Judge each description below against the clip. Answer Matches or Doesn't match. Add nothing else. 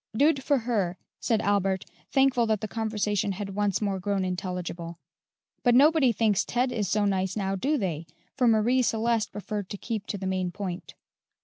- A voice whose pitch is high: Matches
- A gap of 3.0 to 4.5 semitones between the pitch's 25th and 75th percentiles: Matches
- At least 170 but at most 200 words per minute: Matches